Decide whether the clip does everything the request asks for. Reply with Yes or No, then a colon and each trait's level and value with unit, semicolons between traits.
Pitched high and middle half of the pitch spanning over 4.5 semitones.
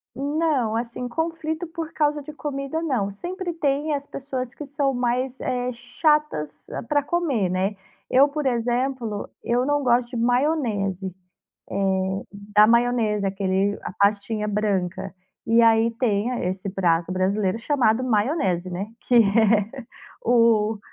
Yes: high, 235 Hz; wide, 5.5 semitones